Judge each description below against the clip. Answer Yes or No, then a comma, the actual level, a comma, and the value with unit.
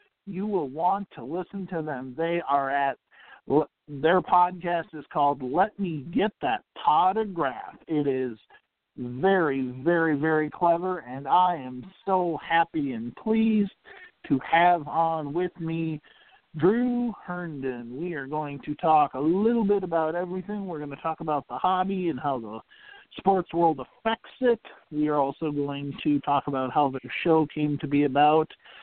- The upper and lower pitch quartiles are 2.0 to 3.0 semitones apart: No, average, 4.5 semitones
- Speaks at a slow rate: No, average, 160 wpm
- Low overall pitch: No, medium, 165 Hz